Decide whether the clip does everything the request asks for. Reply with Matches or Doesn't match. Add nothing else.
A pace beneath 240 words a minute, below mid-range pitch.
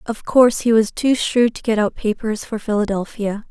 Doesn't match